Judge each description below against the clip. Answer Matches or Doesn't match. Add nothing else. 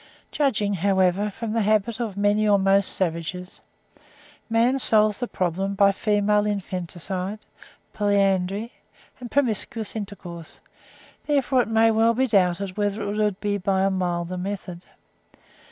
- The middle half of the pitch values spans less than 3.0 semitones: Matches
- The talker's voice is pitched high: Matches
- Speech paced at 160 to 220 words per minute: Doesn't match